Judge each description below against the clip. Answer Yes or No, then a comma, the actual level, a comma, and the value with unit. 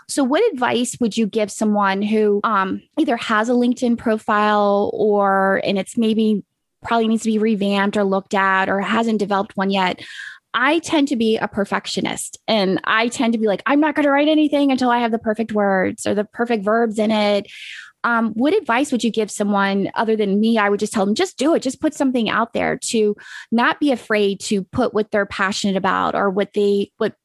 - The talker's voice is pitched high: Yes, high, 215 Hz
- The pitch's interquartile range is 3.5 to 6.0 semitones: No, average, 2.8 semitones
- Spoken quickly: Yes, fast, 215 wpm